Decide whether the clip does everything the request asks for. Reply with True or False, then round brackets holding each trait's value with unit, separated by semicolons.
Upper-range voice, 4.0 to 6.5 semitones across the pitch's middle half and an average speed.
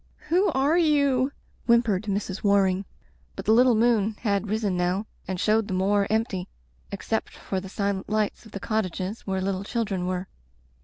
False (205 Hz; 3.1 semitones; 170 wpm)